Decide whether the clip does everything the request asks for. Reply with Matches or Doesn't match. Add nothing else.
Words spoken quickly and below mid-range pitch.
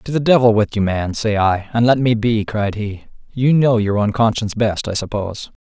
Matches